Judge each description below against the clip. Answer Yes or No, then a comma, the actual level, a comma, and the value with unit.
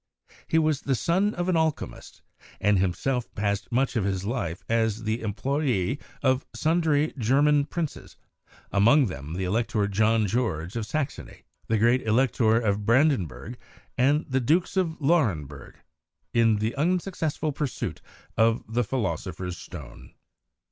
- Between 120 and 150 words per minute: Yes, average, 140 wpm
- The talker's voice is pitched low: Yes, low, 120 Hz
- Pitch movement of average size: No, wide, 6.0 semitones